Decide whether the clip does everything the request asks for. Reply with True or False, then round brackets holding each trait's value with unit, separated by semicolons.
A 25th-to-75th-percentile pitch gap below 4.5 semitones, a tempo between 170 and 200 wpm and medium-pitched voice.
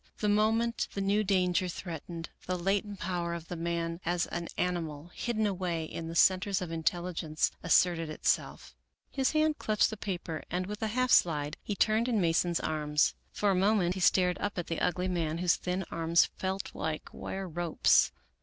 True (3.2 semitones; 180 wpm; 180 Hz)